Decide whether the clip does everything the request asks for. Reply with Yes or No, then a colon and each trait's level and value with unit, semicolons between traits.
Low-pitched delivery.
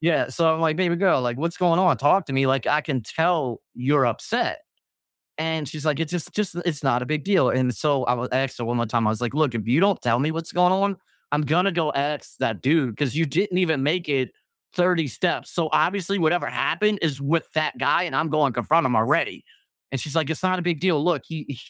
No: medium, 155 Hz